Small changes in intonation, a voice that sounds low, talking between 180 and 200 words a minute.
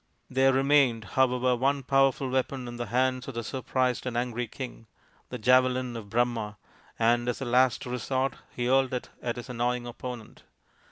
No: narrow, 1.5 semitones; low, 125 Hz; average, 170 wpm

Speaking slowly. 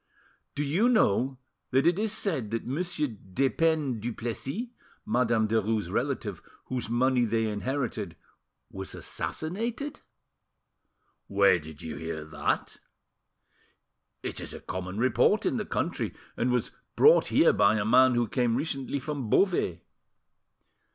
Yes: slow, 130 wpm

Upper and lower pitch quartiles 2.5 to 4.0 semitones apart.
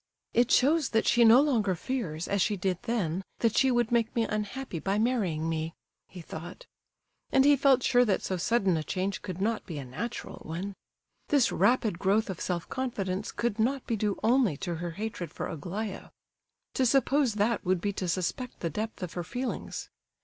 No: average, 5.0 semitones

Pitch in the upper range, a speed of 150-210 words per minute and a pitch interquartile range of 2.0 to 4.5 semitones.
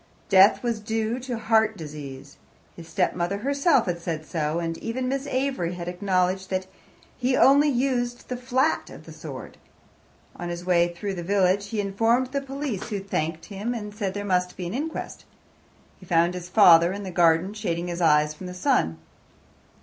No: high, 195 Hz; average, 180 wpm; wide, 5.6 semitones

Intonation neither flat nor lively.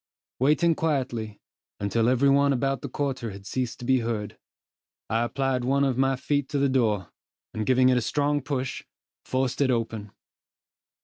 Yes: average, 3.0 semitones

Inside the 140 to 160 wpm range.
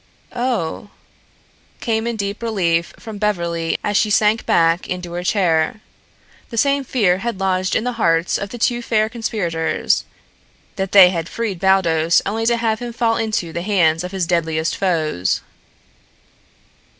Yes: average, 155 wpm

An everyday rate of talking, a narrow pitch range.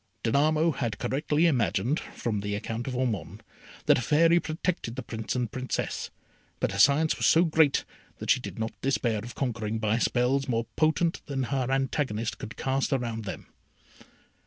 No: average, 170 wpm; average, 4.6 semitones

